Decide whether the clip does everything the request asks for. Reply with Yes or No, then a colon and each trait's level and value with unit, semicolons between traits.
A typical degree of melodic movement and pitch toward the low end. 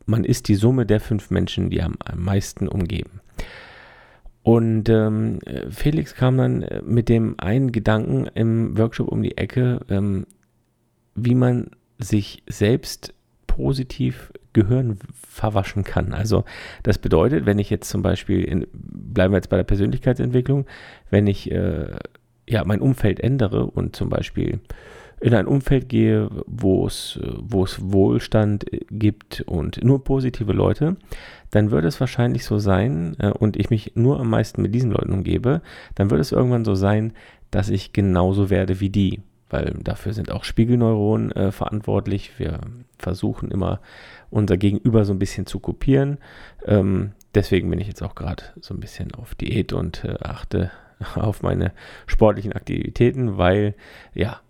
Yes: average, 3.3 semitones; low, 105 Hz